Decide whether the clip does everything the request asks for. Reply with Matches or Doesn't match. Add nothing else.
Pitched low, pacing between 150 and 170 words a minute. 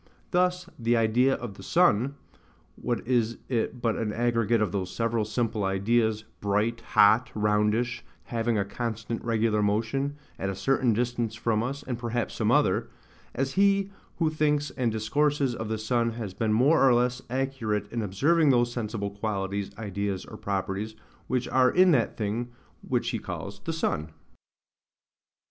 Matches